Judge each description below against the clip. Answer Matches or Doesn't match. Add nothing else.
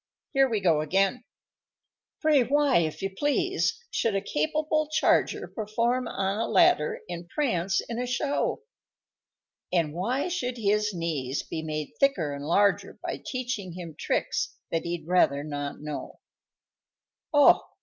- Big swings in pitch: Matches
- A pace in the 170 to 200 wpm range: Doesn't match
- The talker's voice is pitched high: Matches